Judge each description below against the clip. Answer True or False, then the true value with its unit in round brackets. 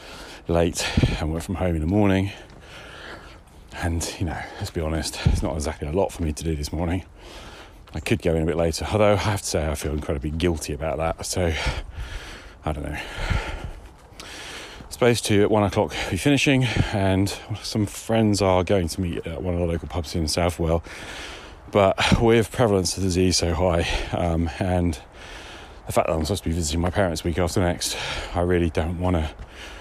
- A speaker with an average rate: True (195 wpm)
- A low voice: True (90 Hz)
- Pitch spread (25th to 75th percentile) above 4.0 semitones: False (3.3 semitones)